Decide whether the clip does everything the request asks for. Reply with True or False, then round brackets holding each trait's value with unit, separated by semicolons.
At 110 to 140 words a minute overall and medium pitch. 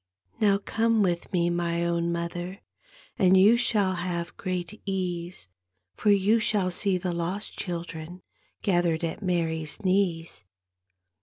True (135 wpm; 180 Hz)